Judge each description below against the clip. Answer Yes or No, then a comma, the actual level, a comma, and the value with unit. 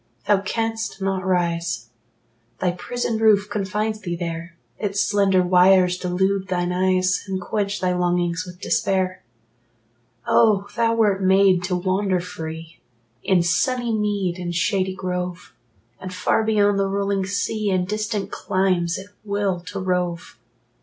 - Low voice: No, high, 190 Hz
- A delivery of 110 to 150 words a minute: Yes, average, 140 wpm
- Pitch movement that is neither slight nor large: No, narrow, 2.1 semitones